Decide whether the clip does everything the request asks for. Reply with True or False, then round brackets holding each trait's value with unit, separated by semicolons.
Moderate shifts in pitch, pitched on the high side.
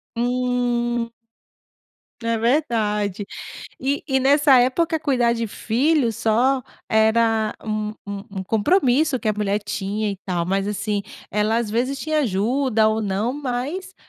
True (3.8 semitones; 230 Hz)